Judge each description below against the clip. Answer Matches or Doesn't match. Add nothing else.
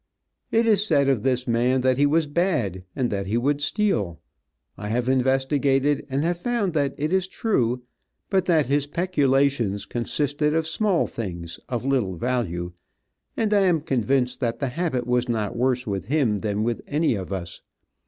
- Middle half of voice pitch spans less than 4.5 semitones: Doesn't match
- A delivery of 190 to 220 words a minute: Doesn't match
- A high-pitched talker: Doesn't match